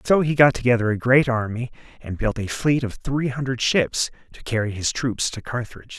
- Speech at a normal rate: No, fast, 210 wpm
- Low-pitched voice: Yes, low, 125 Hz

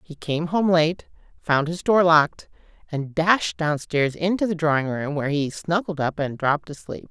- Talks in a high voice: No, medium, 160 Hz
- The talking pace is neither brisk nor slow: Yes, average, 185 wpm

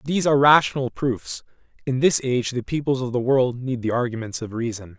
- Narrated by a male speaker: Yes, male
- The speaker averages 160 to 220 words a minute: Yes, fast, 205 wpm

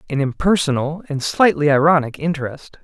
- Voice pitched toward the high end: No, medium, 150 Hz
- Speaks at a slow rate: Yes, slow, 125 wpm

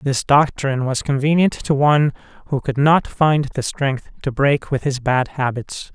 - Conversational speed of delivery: Yes, average, 180 wpm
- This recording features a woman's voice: No, male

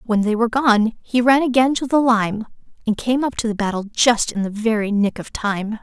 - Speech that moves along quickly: Yes, fast, 235 wpm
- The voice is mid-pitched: No, high, 225 Hz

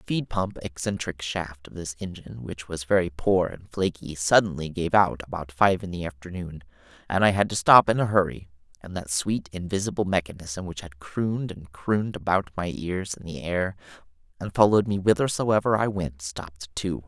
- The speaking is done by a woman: No, male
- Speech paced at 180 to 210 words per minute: Yes, average, 190 wpm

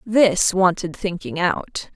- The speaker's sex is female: Yes, female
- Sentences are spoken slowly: Yes, slow, 125 wpm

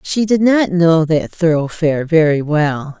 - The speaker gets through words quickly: No, average, 160 wpm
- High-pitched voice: No, medium, 165 Hz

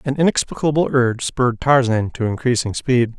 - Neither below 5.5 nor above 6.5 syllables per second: Yes, 5.6 syllables/s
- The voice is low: Yes, low, 125 Hz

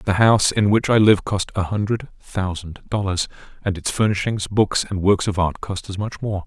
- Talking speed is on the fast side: Yes, fast, 215 wpm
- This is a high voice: No, low, 100 Hz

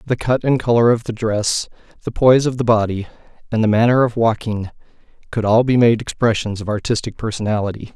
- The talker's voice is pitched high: No, low, 115 Hz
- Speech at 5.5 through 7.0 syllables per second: Yes, 6.0 syllables/s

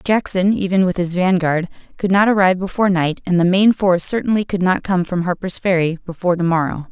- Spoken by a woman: Yes, female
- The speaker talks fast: Yes, fast, 210 wpm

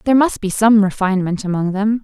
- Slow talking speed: No, fast, 205 wpm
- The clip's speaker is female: Yes, female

